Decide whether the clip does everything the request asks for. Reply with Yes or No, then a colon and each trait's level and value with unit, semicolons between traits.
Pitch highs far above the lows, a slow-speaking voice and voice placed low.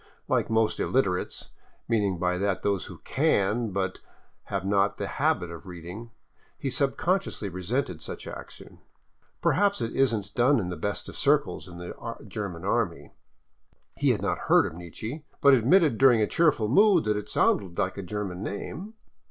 No: wide, 5.8 semitones; average, 170 wpm; low, 105 Hz